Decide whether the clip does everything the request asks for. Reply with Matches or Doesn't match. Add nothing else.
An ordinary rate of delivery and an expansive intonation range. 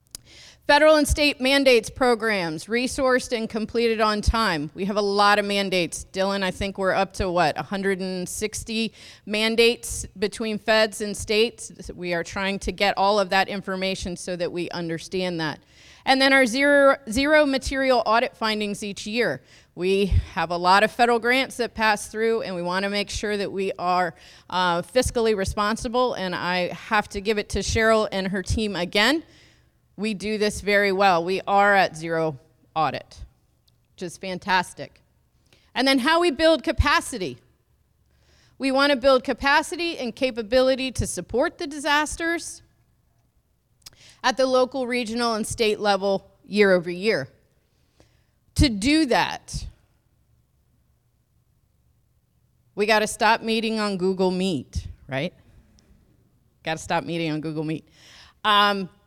Doesn't match